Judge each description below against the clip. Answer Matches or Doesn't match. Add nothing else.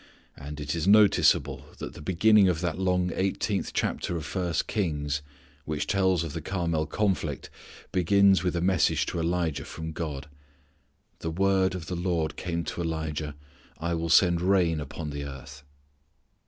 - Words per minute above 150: Matches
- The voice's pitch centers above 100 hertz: Doesn't match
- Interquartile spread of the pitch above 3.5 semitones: Doesn't match